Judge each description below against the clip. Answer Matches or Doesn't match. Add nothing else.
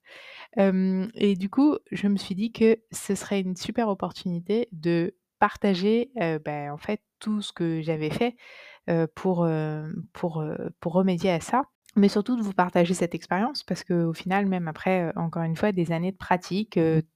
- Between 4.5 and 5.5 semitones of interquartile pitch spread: Doesn't match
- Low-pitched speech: Doesn't match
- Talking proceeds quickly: Doesn't match